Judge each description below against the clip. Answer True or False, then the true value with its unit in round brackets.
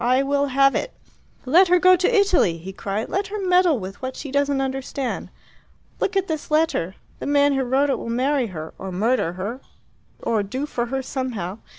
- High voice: True (270 Hz)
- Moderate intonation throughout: True (5.0 semitones)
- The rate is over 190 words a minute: True (200 wpm)